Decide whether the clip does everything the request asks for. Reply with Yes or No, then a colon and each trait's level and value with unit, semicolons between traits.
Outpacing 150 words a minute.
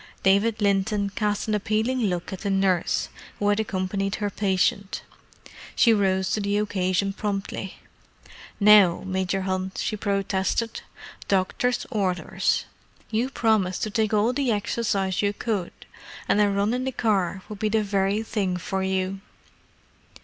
No: average, 145 wpm